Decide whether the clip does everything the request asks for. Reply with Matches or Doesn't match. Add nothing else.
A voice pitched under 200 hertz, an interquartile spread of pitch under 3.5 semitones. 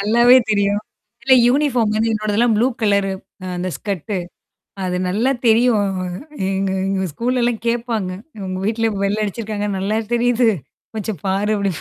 Doesn't match